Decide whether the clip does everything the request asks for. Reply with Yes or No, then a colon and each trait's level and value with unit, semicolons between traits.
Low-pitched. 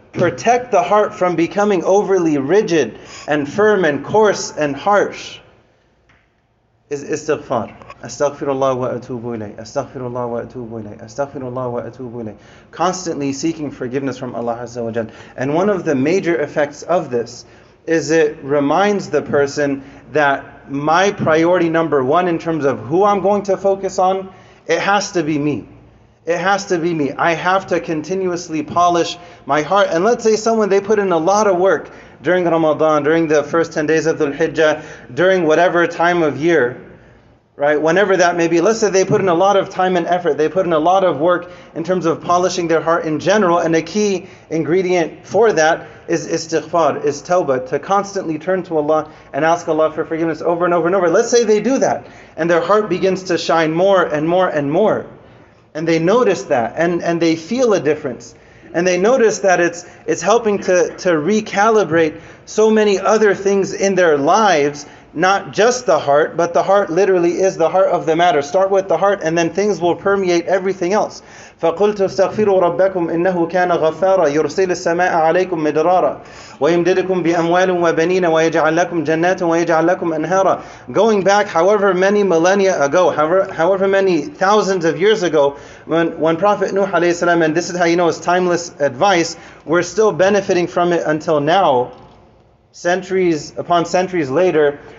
No: medium, 170 Hz